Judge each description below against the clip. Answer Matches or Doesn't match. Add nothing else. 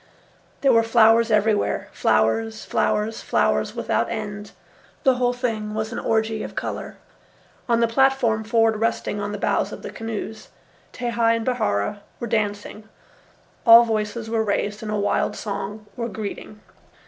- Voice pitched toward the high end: Matches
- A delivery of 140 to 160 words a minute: Matches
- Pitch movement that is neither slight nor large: Doesn't match